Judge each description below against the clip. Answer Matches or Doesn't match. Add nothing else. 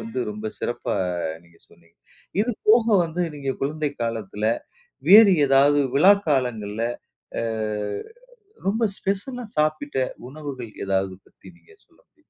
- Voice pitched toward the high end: Doesn't match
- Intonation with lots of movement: Matches